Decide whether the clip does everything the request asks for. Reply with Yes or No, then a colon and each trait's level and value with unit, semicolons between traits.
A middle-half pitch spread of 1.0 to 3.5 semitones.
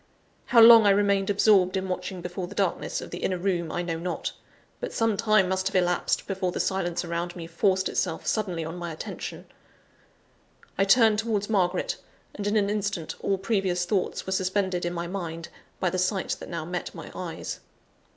Yes: narrow, 2.4 semitones